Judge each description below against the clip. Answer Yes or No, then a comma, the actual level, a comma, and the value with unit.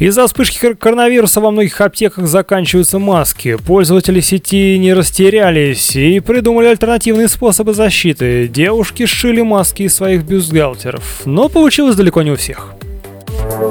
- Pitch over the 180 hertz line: Yes, high, 190 Hz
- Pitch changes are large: Yes, wide, 6.5 semitones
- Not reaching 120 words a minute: No, average, 125 wpm